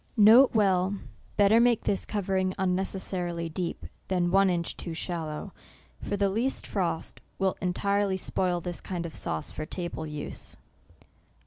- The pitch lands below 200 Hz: Yes, medium, 185 Hz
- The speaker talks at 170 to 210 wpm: No, average, 145 wpm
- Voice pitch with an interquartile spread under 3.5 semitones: Yes, narrow, 2.5 semitones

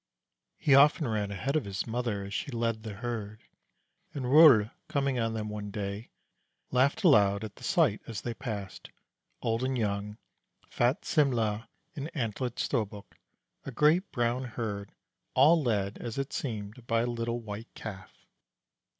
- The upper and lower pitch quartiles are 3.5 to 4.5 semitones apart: Yes, average, 3.9 semitones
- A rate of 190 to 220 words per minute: No, average, 155 wpm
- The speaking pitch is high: No, low, 115 Hz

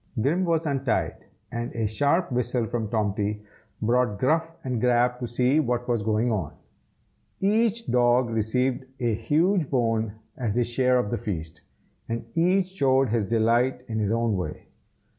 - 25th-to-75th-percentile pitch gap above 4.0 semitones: No, average, 3.2 semitones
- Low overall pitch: Yes, low, 120 Hz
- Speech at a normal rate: Yes, average, 160 wpm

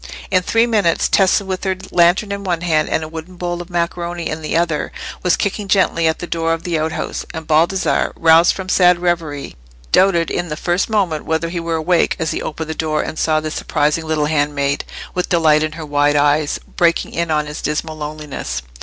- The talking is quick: Yes, fast, 210 wpm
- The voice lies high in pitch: No, medium, 165 Hz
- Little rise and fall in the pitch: Yes, narrow, 2.3 semitones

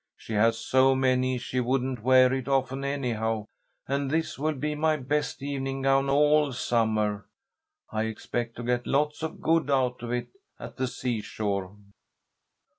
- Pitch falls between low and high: No, low, 130 Hz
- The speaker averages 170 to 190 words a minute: No, average, 155 wpm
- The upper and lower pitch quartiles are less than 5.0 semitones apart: Yes, average, 2.8 semitones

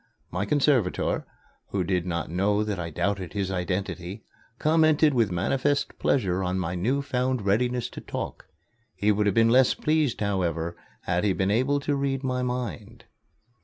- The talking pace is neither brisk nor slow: Yes, average, 165 wpm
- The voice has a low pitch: Yes, low, 105 Hz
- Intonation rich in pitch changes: Yes, wide, 6.0 semitones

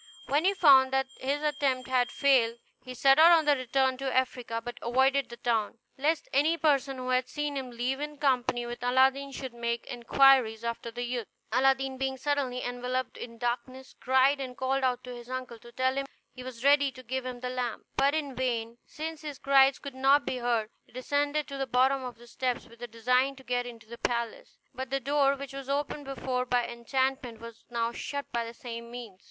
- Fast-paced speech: Yes, fast, 210 wpm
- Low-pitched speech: No, very high, 255 Hz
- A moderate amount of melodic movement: No, narrow, 2.2 semitones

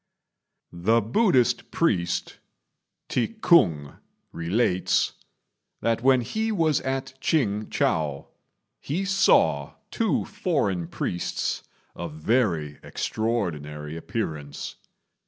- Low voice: Yes, low, 110 Hz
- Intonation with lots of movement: Yes, wide, 8.9 semitones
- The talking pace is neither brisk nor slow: No, slow, 85 wpm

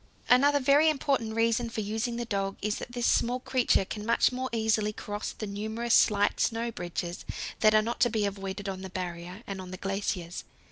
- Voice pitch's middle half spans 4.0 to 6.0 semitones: No, average, 3.3 semitones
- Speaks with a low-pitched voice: No, high, 215 Hz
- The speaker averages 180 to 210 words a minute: Yes, average, 200 wpm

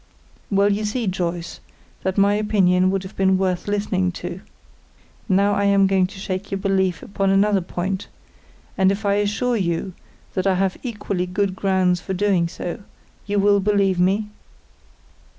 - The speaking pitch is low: No, high, 195 Hz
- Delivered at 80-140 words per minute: No, average, 165 wpm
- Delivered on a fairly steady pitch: Yes, narrow, 1.6 semitones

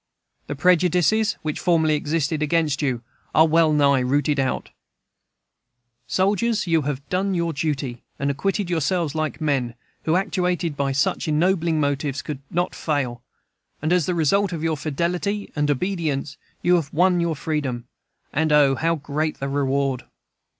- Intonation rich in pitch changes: No, average, 3.6 semitones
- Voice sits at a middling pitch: Yes, medium, 155 Hz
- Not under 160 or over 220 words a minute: No, average, 150 wpm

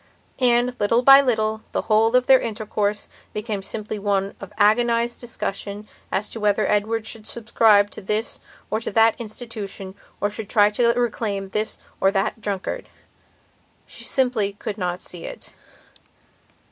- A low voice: No, high, 215 Hz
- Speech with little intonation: Yes, narrow, 2.3 semitones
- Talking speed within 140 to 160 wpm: Yes, average, 145 wpm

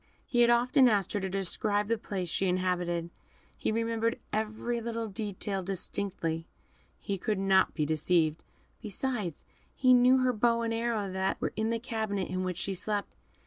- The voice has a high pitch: Yes, high, 205 Hz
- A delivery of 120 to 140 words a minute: No, average, 170 wpm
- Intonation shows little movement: No, average, 3.7 semitones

